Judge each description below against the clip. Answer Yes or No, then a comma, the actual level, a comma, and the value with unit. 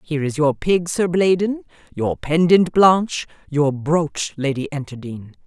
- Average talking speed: Yes, average, 145 wpm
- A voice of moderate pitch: Yes, medium, 155 Hz